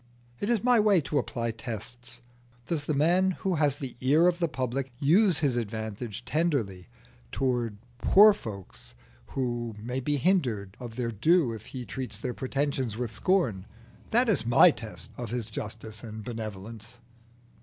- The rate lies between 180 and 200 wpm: No, average, 160 wpm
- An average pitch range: No, wide, 5.8 semitones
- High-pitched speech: No, low, 125 Hz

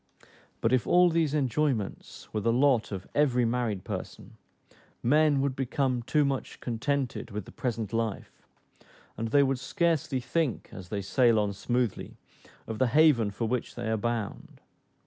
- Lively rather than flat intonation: No, average, 4.0 semitones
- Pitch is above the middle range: No, low, 125 Hz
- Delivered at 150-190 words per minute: Yes, average, 160 wpm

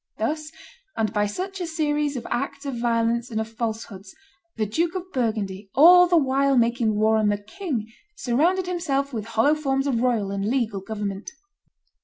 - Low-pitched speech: No, high, 240 Hz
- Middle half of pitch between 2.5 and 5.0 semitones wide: No, wide, 5.4 semitones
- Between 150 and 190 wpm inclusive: Yes, average, 175 wpm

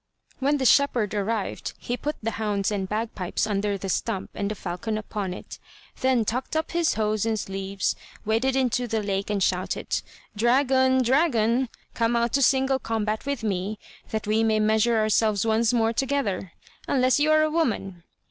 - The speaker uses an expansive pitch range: No, average, 3.9 semitones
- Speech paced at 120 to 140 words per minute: No, average, 175 wpm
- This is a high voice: Yes, high, 225 Hz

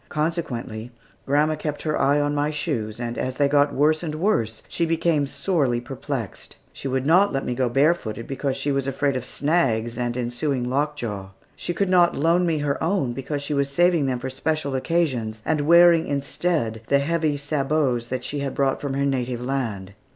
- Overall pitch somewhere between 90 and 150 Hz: Yes, medium, 140 Hz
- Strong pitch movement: No, average, 3.8 semitones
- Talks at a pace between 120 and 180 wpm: No, average, 190 wpm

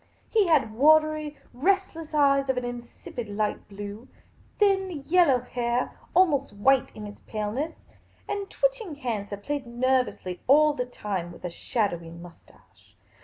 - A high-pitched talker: Yes, very high, 255 Hz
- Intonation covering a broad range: Yes, wide, 6.5 semitones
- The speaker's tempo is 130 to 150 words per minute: No, average, 185 wpm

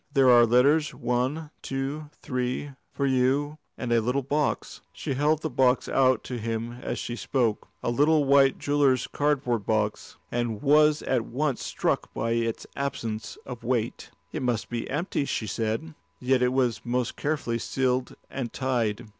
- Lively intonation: No, average, 3.1 semitones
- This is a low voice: Yes, low, 130 Hz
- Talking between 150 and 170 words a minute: Yes, average, 165 wpm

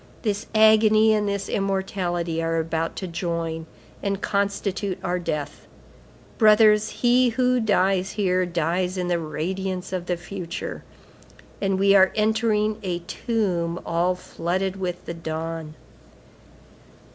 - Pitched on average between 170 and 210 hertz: Yes, high, 190 Hz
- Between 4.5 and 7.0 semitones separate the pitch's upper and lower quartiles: No, average, 3.4 semitones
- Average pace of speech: No, slow, 125 wpm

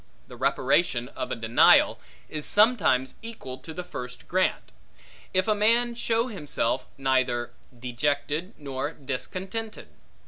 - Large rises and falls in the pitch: Yes, wide, 8.3 semitones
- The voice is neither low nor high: Yes, medium, 150 Hz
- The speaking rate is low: Yes, slow, 125 wpm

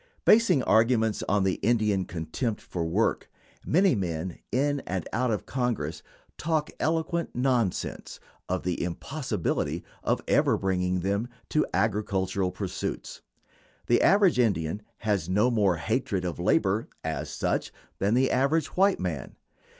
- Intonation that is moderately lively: No, wide, 5.7 semitones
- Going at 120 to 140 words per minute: Yes, slow, 135 wpm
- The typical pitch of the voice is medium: No, low, 105 Hz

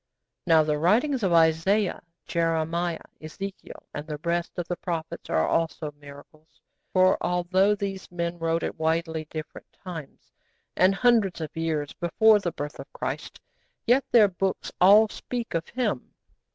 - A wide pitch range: No, average, 3.4 semitones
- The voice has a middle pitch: Yes, medium, 170 Hz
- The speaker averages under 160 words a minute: Yes, average, 150 wpm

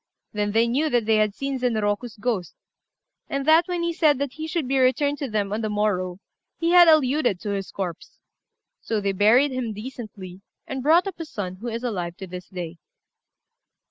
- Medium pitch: No, high, 235 Hz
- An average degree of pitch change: No, wide, 5.8 semitones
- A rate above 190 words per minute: Yes, average, 200 wpm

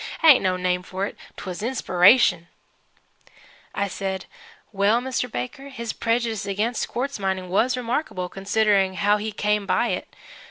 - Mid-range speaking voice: No, high, 210 Hz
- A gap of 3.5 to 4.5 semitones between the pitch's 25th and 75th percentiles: Yes, average, 3.9 semitones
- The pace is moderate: Yes, average, 150 wpm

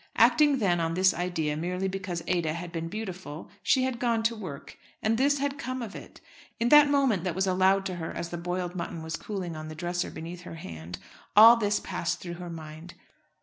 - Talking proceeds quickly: Yes, fast, 215 wpm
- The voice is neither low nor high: Yes, medium, 180 Hz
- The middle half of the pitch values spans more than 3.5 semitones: Yes, average, 4.6 semitones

